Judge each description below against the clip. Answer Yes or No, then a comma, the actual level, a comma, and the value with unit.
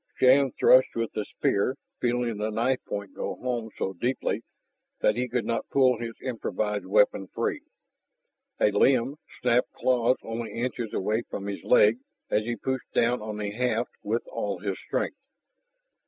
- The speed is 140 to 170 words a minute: Yes, average, 160 wpm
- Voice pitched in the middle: No, low, 115 Hz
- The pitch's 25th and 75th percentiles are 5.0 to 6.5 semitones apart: No, average, 3.1 semitones